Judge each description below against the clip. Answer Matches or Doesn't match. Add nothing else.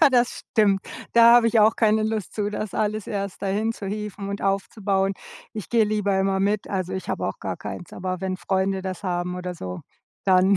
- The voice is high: Matches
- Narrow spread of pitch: Matches